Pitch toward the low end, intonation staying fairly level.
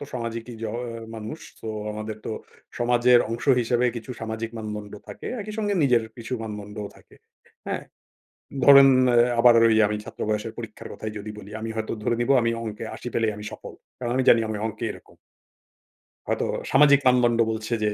Yes: low, 115 Hz; narrow, 2.1 semitones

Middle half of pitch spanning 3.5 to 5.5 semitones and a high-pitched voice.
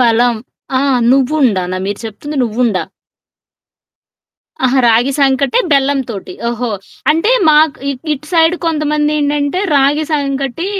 Yes: average, 3.9 semitones; very high, 275 Hz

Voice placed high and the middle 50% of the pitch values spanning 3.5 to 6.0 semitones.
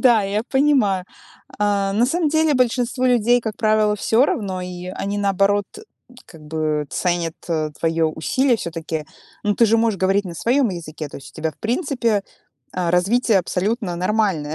Yes: high, 205 Hz; average, 5.0 semitones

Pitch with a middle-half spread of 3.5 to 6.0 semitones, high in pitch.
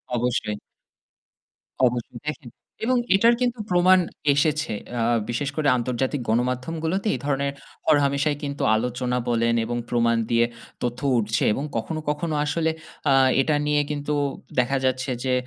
No: average, 4.1 semitones; low, 135 Hz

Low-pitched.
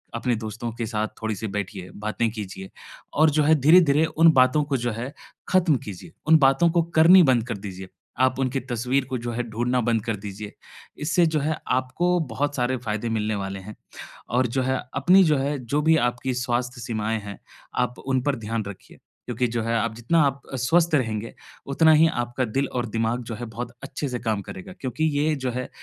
Yes: low, 125 Hz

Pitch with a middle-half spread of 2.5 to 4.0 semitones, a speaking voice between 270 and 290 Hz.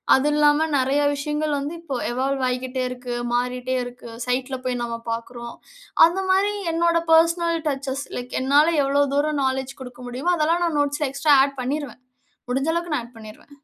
Yes: average, 3.2 semitones; very high, 275 Hz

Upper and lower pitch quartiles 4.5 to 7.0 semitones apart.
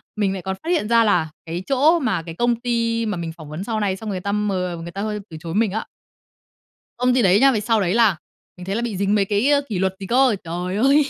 No: average, 3.9 semitones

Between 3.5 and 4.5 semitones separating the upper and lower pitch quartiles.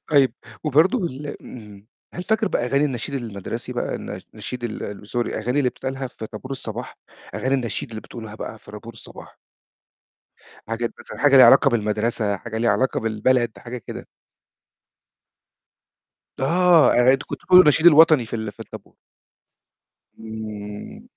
Yes: average, 4.1 semitones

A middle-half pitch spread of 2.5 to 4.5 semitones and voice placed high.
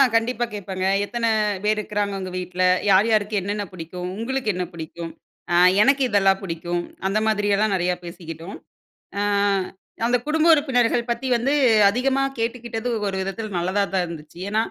Yes: average, 4.1 semitones; high, 205 Hz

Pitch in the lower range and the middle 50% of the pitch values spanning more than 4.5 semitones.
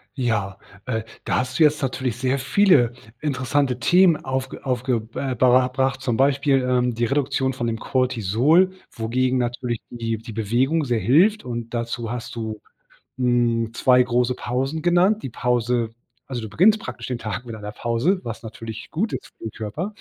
No: low, 125 Hz; average, 2.7 semitones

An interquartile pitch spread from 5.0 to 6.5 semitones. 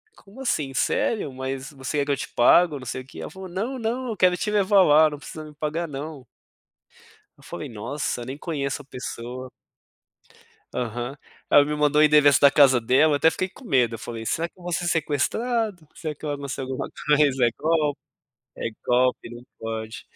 No: average, 4.5 semitones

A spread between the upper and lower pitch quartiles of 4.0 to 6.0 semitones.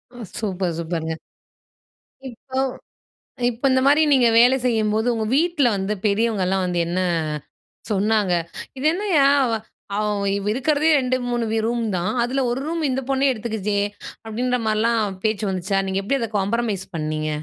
Yes: average, 4.4 semitones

